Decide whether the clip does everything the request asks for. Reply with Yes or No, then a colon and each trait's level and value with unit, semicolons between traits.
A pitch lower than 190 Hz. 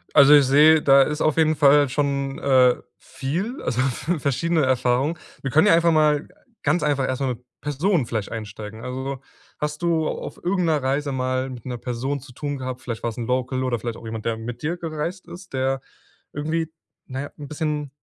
Yes: medium, 140 Hz